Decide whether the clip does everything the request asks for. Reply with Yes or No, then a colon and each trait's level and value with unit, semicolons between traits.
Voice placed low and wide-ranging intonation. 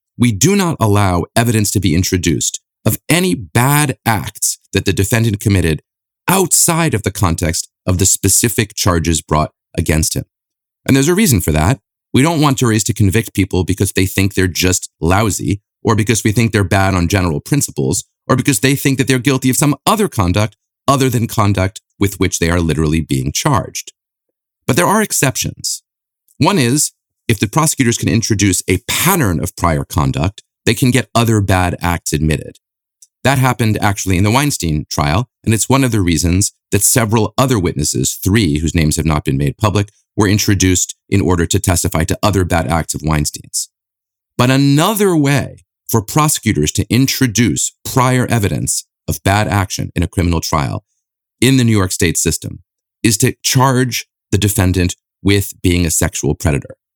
Yes: low, 105 Hz; wide, 5.7 semitones